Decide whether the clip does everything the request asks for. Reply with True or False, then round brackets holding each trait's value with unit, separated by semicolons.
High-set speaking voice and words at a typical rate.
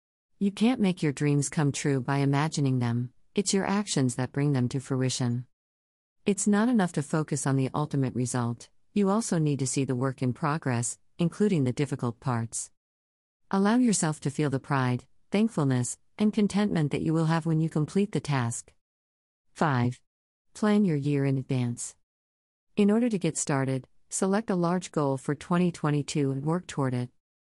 False (140 Hz; 175 wpm)